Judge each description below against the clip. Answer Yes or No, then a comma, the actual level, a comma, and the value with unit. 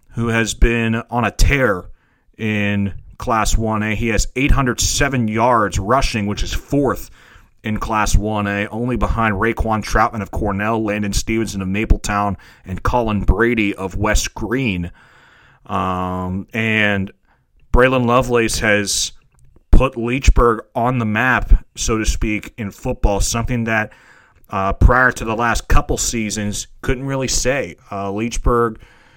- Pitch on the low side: Yes, low, 110 Hz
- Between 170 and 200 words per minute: No, average, 140 wpm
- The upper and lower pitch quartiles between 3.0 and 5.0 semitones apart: No, narrow, 2.6 semitones